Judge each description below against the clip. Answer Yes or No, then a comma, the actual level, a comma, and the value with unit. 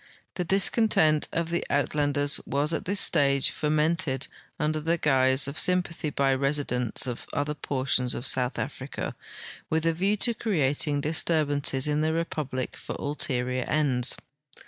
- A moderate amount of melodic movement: Yes, average, 3.2 semitones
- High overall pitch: No, medium, 150 Hz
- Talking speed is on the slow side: No, average, 145 wpm